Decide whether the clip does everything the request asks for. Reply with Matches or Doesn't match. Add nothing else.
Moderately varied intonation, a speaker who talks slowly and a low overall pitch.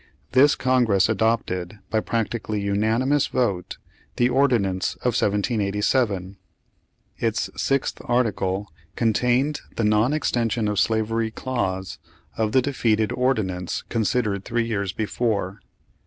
Matches